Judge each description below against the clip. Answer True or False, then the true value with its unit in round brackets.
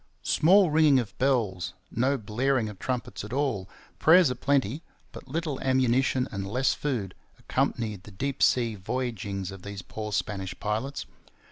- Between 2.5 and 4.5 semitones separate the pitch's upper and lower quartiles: False (5.1 semitones)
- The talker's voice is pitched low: True (120 Hz)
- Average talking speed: True (150 wpm)